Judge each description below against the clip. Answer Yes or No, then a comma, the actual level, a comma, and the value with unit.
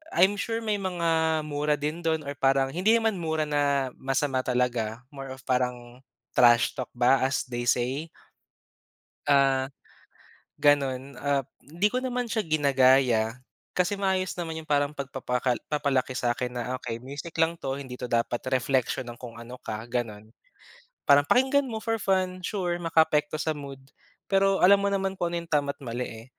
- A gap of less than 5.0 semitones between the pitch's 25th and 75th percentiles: No, average, 5.3 semitones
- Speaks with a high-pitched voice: No, medium, 145 Hz